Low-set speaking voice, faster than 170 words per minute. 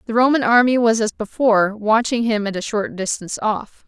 No: high, 220 Hz; average, 200 wpm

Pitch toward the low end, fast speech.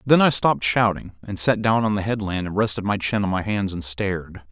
Yes: low, 100 Hz; fast, 255 wpm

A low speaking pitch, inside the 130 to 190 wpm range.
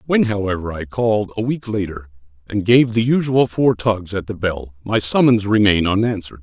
Yes: low, 105 Hz; average, 185 wpm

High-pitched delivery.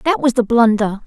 Yes: high, 240 Hz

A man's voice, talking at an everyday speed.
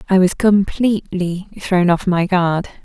No: female; average, 150 wpm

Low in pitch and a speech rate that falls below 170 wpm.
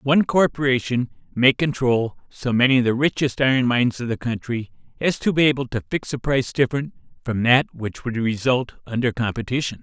No: low, 125 Hz; average, 185 wpm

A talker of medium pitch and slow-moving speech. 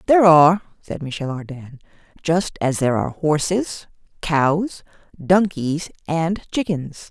Yes: medium, 160 Hz; slow, 120 wpm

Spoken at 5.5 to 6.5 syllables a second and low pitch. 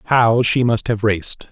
No: 4.6 syllables/s; low, 115 Hz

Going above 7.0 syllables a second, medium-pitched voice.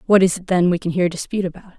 Yes: 8.7 syllables/s; medium, 180 Hz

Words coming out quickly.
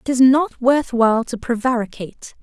No: average, 175 wpm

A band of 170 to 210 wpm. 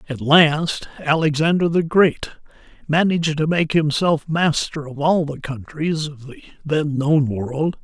No: average, 145 wpm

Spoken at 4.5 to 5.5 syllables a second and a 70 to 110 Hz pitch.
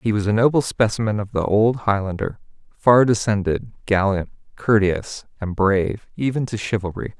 Yes: 5.0 syllables/s; low, 105 Hz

